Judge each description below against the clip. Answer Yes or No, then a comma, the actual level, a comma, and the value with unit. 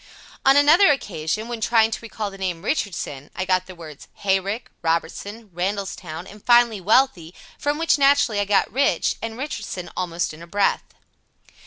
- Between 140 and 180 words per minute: Yes, average, 170 wpm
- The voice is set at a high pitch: Yes, high, 205 Hz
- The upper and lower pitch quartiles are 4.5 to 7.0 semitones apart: Yes, average, 5.0 semitones